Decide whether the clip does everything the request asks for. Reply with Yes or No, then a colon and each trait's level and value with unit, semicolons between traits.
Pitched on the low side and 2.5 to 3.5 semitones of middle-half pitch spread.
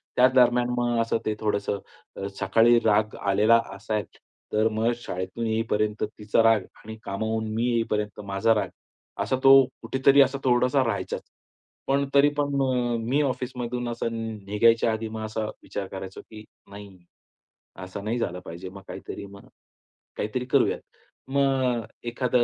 Yes: low, 115 Hz; average, 2.9 semitones